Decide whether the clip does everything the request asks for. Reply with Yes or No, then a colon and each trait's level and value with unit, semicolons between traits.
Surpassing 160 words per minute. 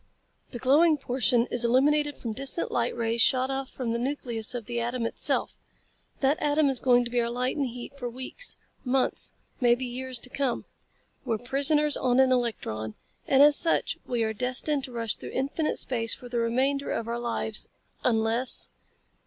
Yes: average, 180 wpm